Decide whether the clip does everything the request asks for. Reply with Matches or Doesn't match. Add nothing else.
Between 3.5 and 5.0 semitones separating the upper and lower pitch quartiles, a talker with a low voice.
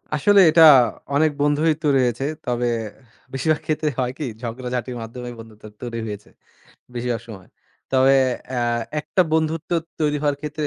Matches